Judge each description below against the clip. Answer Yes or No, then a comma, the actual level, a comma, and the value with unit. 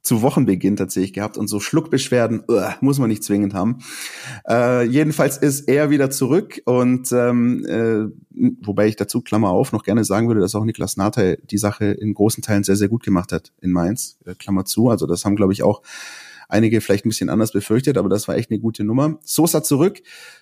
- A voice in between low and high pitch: No, low, 110 Hz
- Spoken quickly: Yes, fast, 210 wpm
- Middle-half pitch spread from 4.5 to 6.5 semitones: No, average, 3.8 semitones